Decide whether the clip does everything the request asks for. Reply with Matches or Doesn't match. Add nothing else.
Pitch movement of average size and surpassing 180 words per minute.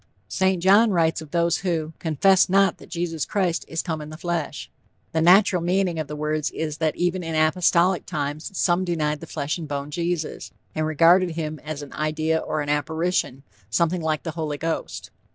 Doesn't match